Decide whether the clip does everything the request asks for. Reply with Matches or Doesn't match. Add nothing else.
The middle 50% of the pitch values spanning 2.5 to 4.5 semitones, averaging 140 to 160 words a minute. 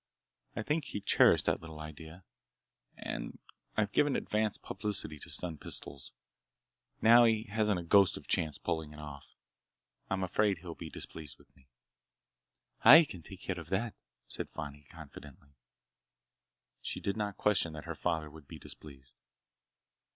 Doesn't match